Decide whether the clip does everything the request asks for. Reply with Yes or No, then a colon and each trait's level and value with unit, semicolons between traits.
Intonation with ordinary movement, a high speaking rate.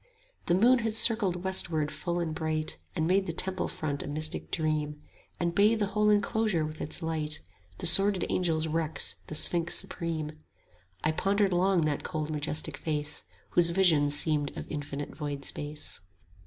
No: average, 3.7 semitones; average, 170 wpm